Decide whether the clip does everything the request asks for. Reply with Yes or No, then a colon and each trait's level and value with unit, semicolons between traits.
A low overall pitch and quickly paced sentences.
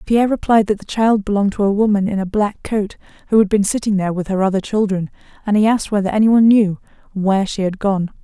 No: high, 205 Hz; fast, 235 wpm